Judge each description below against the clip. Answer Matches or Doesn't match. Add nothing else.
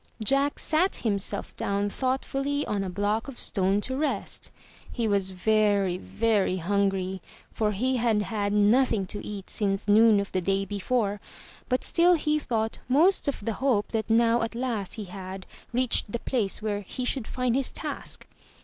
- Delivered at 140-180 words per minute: Matches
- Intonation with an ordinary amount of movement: Matches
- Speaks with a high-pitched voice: Matches